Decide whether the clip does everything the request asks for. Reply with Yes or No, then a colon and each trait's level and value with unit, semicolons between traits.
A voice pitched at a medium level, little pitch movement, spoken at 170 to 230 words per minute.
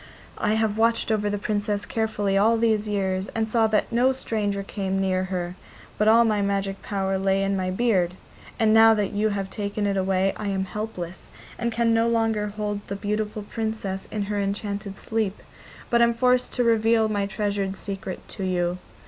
No: high, 205 Hz; narrow, 2.2 semitones; average, 190 wpm